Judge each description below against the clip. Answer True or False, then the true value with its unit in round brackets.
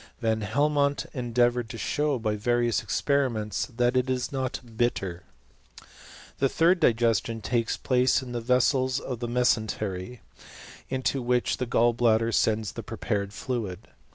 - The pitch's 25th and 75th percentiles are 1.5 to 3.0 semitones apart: True (2.5 semitones)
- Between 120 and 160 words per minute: True (150 wpm)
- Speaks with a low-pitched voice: True (120 Hz)